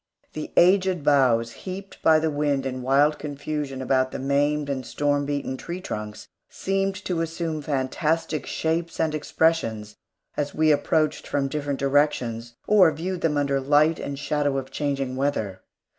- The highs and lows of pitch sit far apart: No, average, 2.8 semitones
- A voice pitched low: No, medium, 145 Hz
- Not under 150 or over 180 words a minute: Yes, average, 155 wpm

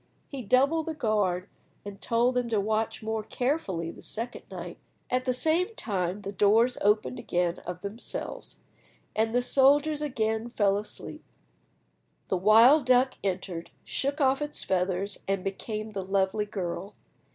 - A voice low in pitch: No, high, 220 Hz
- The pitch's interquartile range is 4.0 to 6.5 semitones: Yes, average, 4.5 semitones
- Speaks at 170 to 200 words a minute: No, average, 150 wpm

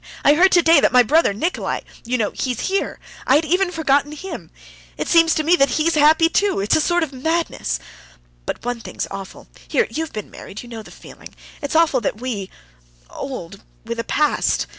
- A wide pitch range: Yes, wide, 6.4 semitones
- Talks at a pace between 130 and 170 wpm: No, average, 190 wpm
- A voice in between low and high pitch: No, very high, 285 Hz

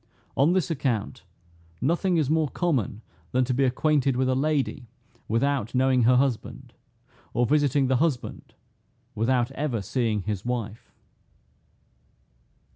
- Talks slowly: Yes, slow, 125 wpm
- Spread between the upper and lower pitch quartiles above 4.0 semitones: No, average, 3.3 semitones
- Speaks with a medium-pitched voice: No, low, 130 Hz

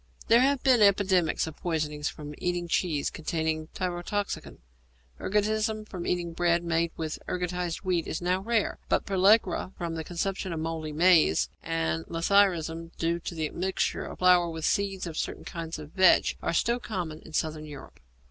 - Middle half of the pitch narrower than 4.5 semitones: Yes, average, 3.0 semitones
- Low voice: No, medium, 175 Hz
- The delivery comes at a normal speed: Yes, average, 170 wpm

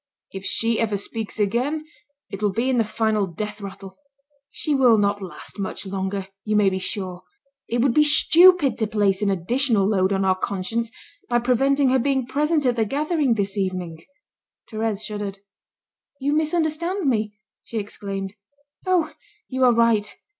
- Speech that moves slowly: No, average, 165 wpm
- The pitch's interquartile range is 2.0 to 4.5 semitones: No, average, 5.1 semitones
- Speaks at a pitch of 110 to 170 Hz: No, high, 220 Hz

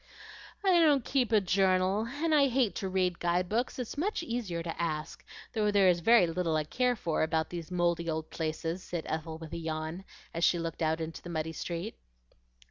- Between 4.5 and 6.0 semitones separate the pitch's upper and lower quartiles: Yes, wide, 5.5 semitones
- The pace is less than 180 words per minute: No, fast, 205 wpm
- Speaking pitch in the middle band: Yes, medium, 175 Hz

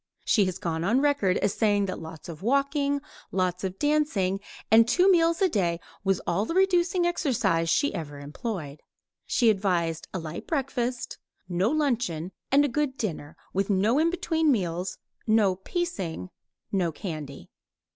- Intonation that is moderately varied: No, wide, 8.4 semitones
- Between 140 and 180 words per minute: Yes, average, 155 wpm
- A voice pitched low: No, high, 205 Hz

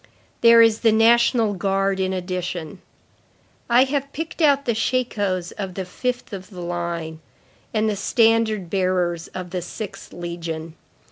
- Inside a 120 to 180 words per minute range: Yes, average, 145 wpm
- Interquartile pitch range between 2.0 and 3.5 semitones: No, average, 4.4 semitones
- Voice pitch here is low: No, high, 195 Hz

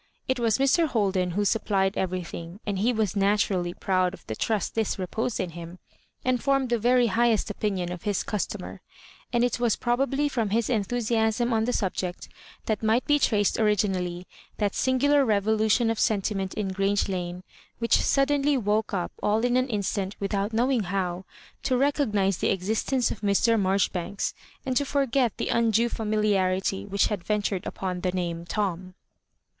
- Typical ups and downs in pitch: Yes, average, 3.9 semitones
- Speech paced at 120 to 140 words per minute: No, average, 175 wpm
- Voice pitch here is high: Yes, high, 210 Hz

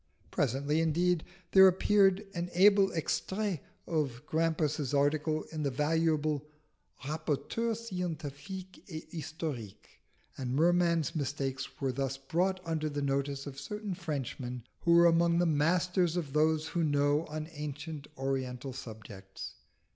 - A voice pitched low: No, medium, 155 Hz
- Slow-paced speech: Yes, slow, 125 wpm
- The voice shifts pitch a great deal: No, average, 3.7 semitones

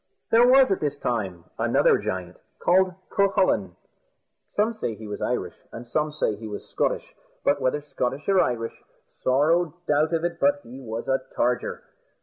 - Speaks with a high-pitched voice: No, medium, 145 Hz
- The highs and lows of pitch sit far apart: Yes, wide, 6.9 semitones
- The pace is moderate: Yes, average, 165 wpm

